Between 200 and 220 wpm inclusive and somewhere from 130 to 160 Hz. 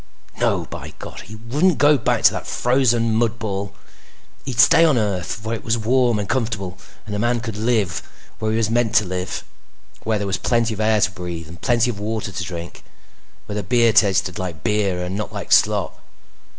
No: fast, 205 wpm; low, 110 Hz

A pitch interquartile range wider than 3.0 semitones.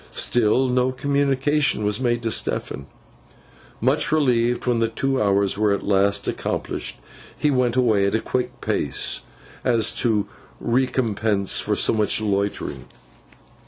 Yes: average, 3.8 semitones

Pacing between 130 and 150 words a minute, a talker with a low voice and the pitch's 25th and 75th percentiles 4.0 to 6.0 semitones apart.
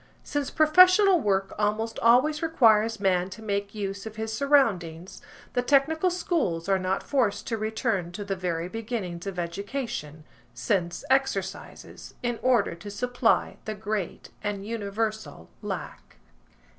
No: slow, 135 wpm; high, 215 Hz; average, 4.4 semitones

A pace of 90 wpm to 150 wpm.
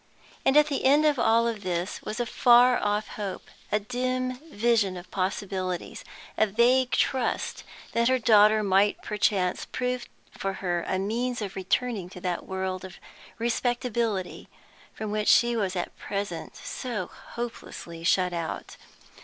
Yes: average, 145 wpm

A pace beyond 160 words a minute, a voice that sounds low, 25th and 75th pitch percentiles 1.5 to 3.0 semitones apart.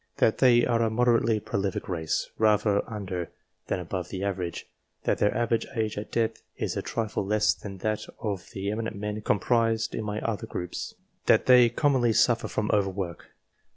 Yes: average, 180 wpm; low, 105 Hz; average, 2.7 semitones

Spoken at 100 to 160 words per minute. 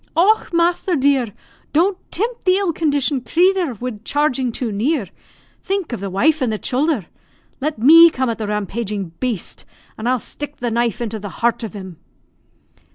No: average, 170 wpm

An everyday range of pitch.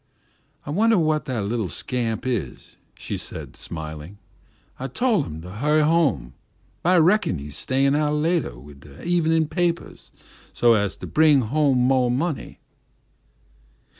No: wide, 7.7 semitones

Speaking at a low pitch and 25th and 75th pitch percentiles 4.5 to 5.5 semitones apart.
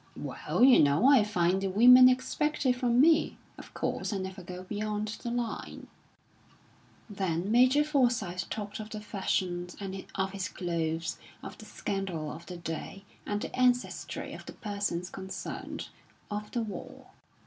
No: high, 205 Hz; average, 4.8 semitones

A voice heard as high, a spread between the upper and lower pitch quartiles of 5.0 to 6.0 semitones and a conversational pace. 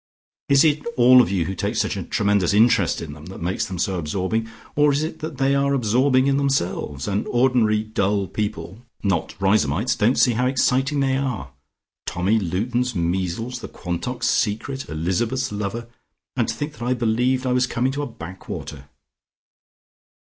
No: low, 115 Hz; wide, 5.4 semitones; average, 175 wpm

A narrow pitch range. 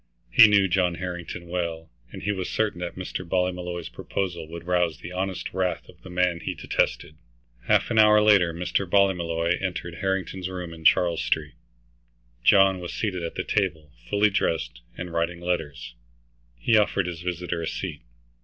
Yes: narrow, 2.1 semitones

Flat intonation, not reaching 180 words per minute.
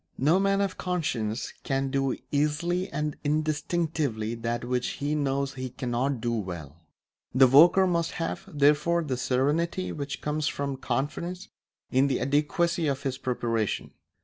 No: average, 4.2 semitones; average, 145 wpm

